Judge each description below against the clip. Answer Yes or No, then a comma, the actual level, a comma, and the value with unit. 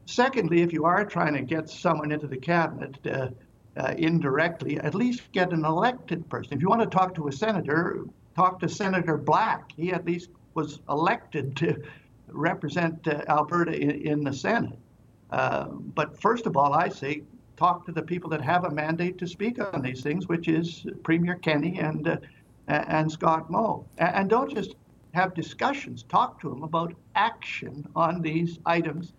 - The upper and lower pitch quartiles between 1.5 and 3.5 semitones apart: Yes, average, 2.8 semitones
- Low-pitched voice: No, medium, 165 Hz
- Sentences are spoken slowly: No, average, 180 wpm